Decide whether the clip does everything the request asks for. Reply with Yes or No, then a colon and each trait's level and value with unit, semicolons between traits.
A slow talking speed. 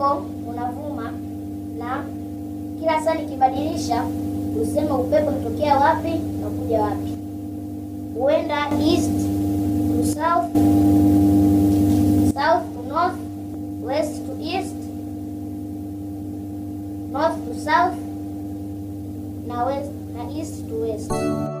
Yes: slow, 80 wpm